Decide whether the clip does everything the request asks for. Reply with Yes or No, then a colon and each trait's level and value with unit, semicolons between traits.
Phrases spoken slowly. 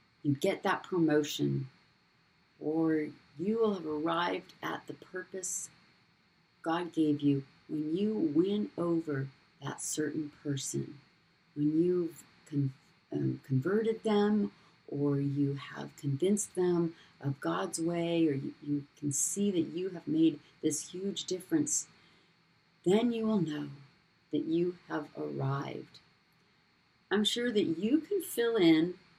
Yes: slow, 130 wpm